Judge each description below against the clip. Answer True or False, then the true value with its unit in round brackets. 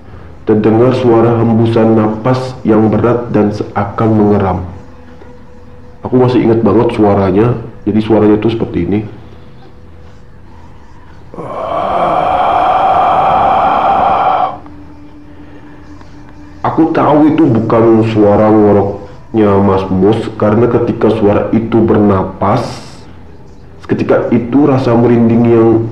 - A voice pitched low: True (110 Hz)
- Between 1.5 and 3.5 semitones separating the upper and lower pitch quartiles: True (3.1 semitones)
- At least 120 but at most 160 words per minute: False (85 wpm)